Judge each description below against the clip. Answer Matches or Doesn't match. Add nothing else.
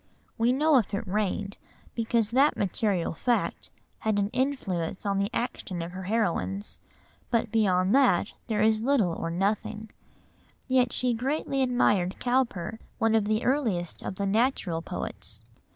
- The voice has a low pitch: Doesn't match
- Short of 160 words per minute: Matches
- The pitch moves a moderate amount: Matches